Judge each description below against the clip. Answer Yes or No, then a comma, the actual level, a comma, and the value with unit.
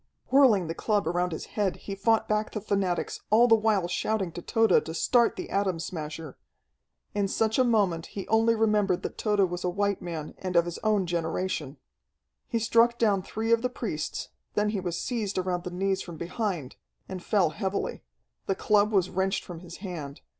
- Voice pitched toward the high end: Yes, high, 195 Hz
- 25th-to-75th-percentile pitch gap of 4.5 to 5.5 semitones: No, average, 3.6 semitones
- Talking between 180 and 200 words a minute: Yes, average, 195 wpm